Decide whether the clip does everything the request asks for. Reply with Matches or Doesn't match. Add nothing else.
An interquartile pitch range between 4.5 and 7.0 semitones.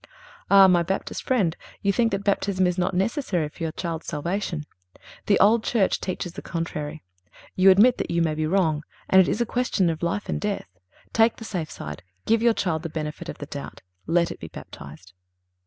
Doesn't match